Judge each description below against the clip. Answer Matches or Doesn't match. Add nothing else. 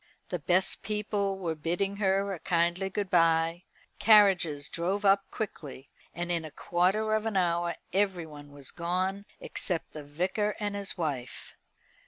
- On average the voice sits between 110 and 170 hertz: Doesn't match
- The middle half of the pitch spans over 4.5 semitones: Doesn't match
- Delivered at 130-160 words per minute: Matches